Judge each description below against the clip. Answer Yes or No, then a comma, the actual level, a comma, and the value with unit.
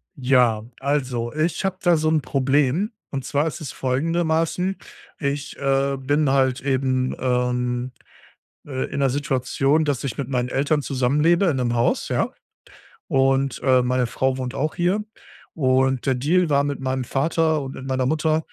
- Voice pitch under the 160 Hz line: Yes, low, 135 Hz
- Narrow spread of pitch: No, average, 3.0 semitones